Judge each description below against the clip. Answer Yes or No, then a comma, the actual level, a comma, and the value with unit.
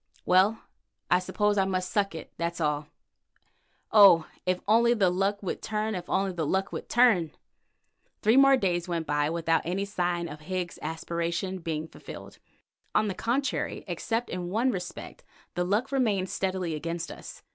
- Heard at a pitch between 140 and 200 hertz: Yes, medium, 185 Hz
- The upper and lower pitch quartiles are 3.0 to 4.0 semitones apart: Yes, average, 3.6 semitones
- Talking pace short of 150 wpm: No, average, 165 wpm